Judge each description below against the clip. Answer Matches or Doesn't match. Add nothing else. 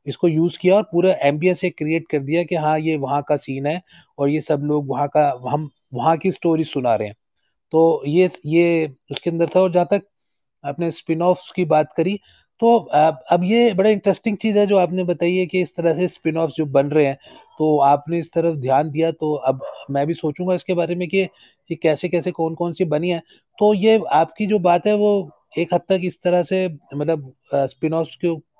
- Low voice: Doesn't match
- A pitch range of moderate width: Matches